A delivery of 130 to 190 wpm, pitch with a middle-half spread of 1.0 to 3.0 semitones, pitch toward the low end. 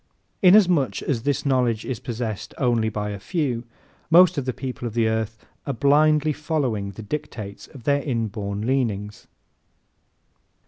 No: average, 145 wpm; average, 4.5 semitones; low, 125 Hz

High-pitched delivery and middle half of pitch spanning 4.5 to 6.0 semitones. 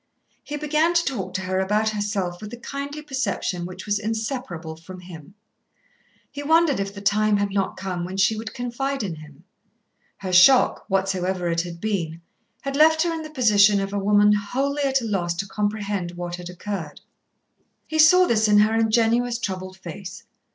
Yes: high, 205 Hz; average, 4.8 semitones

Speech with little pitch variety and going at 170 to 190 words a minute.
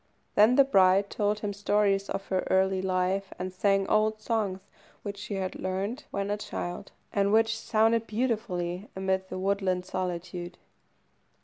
No: narrow, 2.1 semitones; average, 150 wpm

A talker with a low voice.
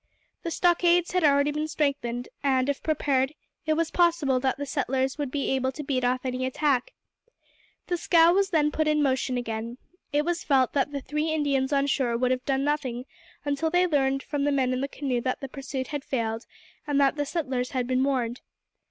No: very high, 275 Hz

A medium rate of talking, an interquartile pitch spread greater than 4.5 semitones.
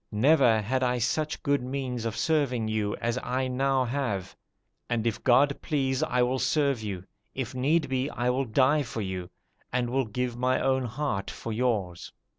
No: average, 180 wpm; average, 2.8 semitones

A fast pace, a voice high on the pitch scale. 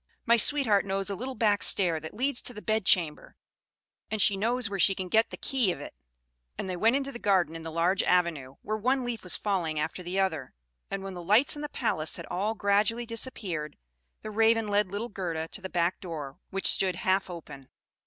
Yes: fast, 215 wpm; high, 195 Hz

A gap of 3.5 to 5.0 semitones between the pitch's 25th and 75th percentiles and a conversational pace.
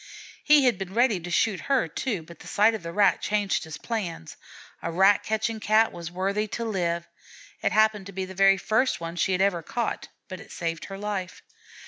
No: average, 3.8 semitones; fast, 210 wpm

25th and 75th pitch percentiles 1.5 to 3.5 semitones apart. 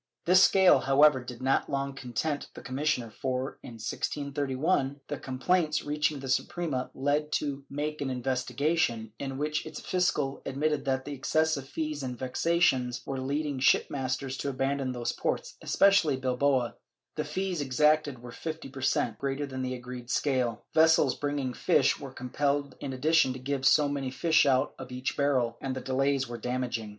Yes: narrow, 2.5 semitones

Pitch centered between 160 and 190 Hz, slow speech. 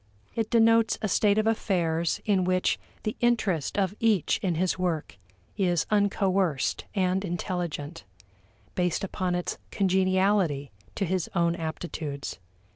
Yes: medium, 185 Hz; slow, 125 wpm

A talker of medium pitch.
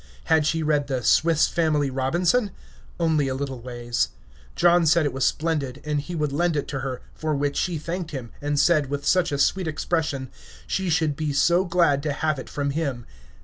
Yes: medium, 150 Hz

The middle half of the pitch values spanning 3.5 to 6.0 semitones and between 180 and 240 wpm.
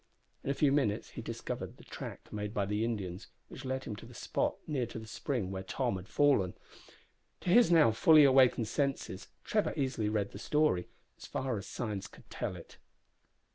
Yes: average, 5.2 semitones; average, 195 wpm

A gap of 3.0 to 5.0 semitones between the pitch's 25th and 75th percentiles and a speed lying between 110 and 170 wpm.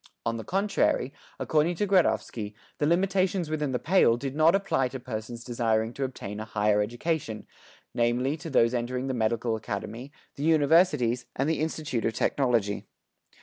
No: wide, 5.4 semitones; average, 160 wpm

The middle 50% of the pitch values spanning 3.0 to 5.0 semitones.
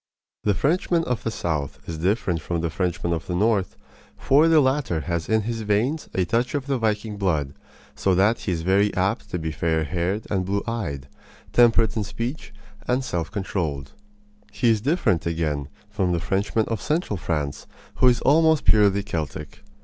No: wide, 5.5 semitones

